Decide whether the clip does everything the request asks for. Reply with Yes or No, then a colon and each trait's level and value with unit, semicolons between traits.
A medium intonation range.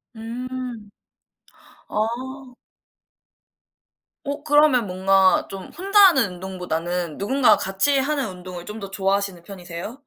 No: wide, 5.7 semitones